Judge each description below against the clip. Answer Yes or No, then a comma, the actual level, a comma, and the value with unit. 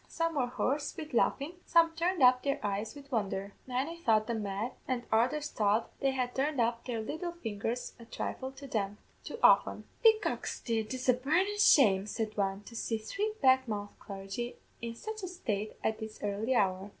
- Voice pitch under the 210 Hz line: No, high, 245 Hz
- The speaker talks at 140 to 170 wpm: No, average, 185 wpm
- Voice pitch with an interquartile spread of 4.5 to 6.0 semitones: Yes, average, 5.2 semitones